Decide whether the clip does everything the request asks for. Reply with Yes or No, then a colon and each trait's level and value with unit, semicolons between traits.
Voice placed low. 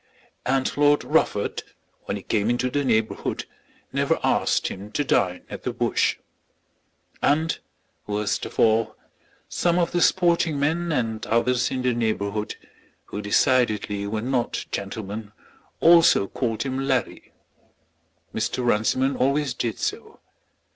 Yes: low, 120 Hz